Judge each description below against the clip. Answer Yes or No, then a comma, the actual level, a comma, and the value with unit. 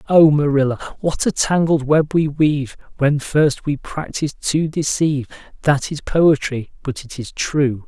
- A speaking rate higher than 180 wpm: No, average, 160 wpm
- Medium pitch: Yes, medium, 145 Hz